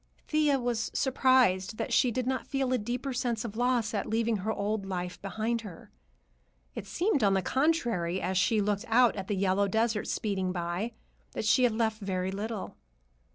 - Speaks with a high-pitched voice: Yes, high, 220 Hz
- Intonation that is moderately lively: Yes, average, 4.1 semitones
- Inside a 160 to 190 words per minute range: Yes, average, 185 wpm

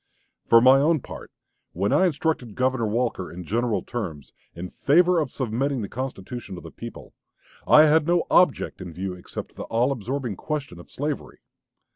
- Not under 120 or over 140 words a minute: No, average, 170 wpm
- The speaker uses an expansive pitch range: Yes, wide, 6.3 semitones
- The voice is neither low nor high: No, low, 125 Hz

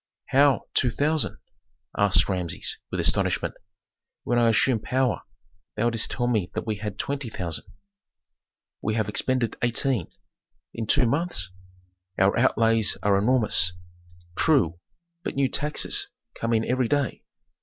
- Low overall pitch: Yes, low, 115 Hz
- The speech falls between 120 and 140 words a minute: Yes, slow, 135 wpm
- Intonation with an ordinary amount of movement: Yes, average, 4.0 semitones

